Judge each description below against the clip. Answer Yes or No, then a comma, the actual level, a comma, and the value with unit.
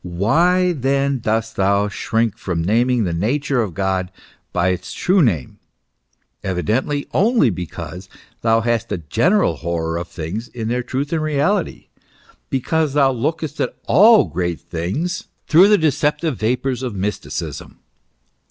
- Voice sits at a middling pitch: No, low, 120 Hz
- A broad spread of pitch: Yes, wide, 7.9 semitones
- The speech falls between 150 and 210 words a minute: No, slow, 135 wpm